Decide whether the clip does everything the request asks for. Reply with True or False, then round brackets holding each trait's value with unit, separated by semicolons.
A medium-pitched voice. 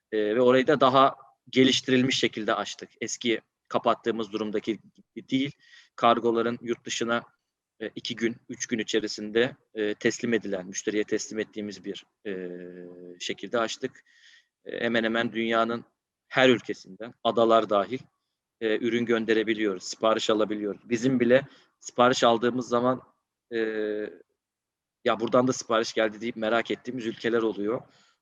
False (115 Hz)